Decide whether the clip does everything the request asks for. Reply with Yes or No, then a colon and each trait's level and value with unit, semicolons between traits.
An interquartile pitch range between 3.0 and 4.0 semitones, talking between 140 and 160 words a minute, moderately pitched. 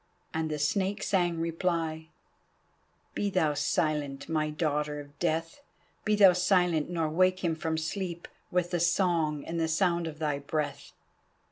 No: narrow, 2.6 semitones; average, 150 wpm; medium, 165 Hz